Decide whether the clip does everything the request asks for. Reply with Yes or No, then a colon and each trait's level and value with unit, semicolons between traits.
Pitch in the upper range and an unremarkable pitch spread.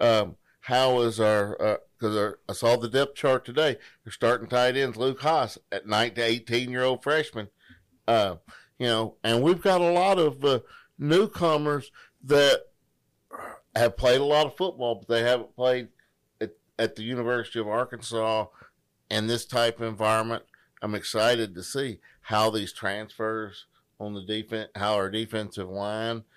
No: low, 115 Hz; average, 3.0 semitones